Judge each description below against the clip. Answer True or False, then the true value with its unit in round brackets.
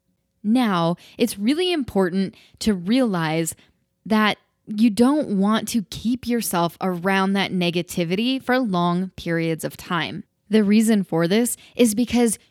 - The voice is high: True (210 Hz)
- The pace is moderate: False (130 wpm)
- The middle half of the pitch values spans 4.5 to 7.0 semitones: True (4.9 semitones)